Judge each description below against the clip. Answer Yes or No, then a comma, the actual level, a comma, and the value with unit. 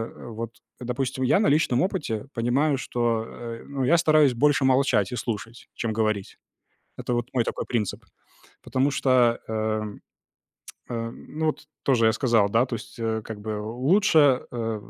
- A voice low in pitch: Yes, low, 120 Hz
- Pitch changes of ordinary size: Yes, average, 3.2 semitones